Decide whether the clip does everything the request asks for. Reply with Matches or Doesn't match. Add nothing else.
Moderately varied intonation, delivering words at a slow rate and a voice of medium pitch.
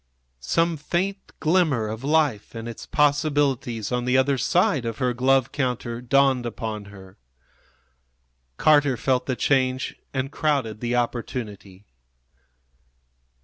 Doesn't match